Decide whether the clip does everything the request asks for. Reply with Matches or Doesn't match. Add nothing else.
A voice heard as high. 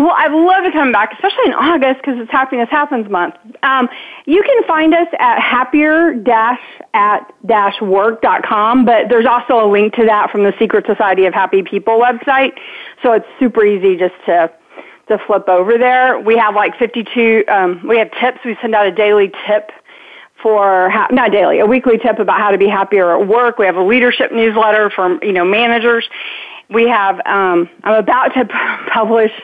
Matches